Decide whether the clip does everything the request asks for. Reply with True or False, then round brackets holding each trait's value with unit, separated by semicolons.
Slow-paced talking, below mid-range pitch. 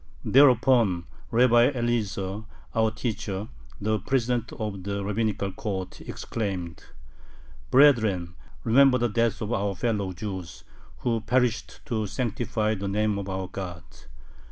True (120 wpm; 110 Hz)